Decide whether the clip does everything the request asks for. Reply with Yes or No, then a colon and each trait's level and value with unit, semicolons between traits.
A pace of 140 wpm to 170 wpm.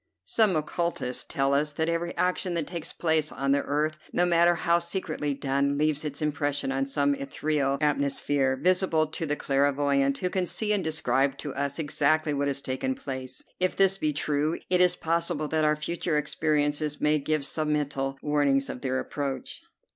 No: average, 180 wpm